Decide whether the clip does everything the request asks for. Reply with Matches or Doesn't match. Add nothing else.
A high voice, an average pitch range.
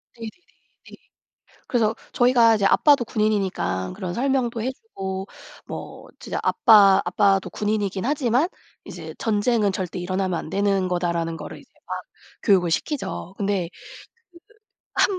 Matches